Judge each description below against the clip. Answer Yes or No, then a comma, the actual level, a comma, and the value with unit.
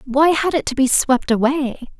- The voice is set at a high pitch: Yes, very high, 275 Hz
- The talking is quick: Yes, fast, 210 wpm